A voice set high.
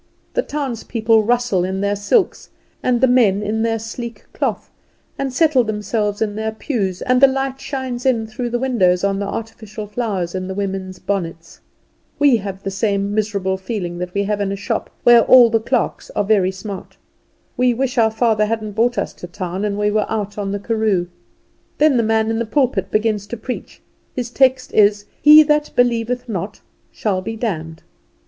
Yes: high, 220 Hz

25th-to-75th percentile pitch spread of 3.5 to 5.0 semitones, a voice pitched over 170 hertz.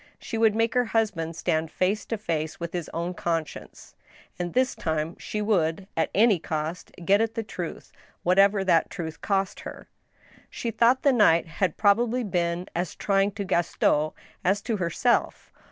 Yes: average, 4.7 semitones; high, 190 Hz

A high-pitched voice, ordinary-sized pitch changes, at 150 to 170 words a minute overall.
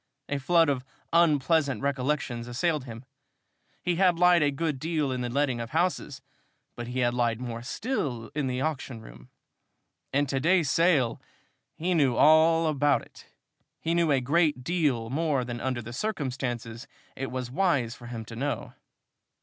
No: low, 135 Hz; average, 4.8 semitones; average, 165 wpm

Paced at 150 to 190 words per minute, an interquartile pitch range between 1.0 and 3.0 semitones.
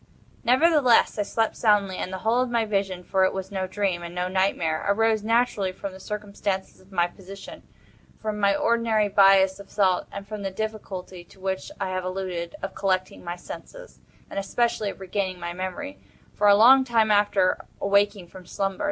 Yes: average, 175 wpm; narrow, 2.4 semitones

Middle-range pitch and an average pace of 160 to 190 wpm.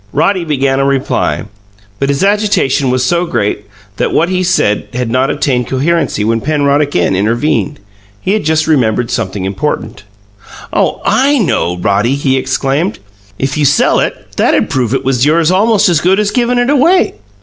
Yes: medium, 145 Hz; average, 170 wpm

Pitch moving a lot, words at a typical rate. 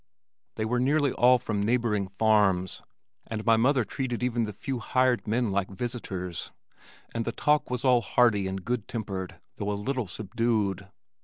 No: average, 3.6 semitones; average, 165 wpm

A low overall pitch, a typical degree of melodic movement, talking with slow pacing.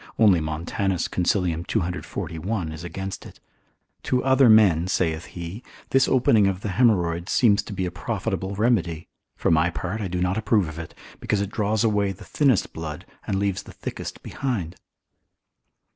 No: very low, 95 Hz; average, 4.0 semitones; average, 165 wpm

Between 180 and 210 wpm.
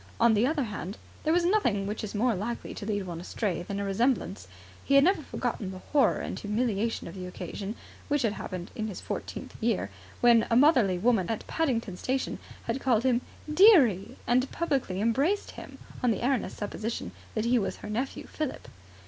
Yes: average, 190 wpm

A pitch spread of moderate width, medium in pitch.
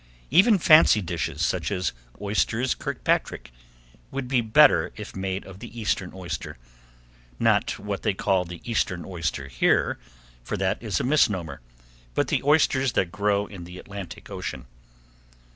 No: average, 4.8 semitones; low, 100 Hz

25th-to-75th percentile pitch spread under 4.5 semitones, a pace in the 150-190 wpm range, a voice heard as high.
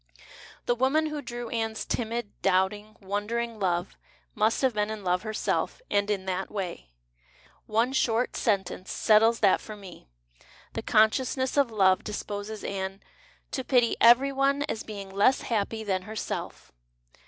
Yes: average, 3.2 semitones; average, 155 wpm; high, 215 Hz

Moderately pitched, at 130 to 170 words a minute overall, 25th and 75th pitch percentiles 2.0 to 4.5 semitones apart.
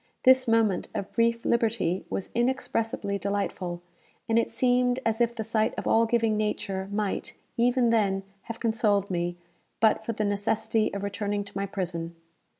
No: high, 220 Hz; average, 160 wpm; narrow, 2.6 semitones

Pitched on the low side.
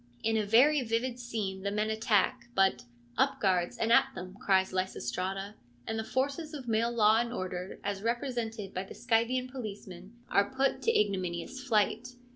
No: high, 220 Hz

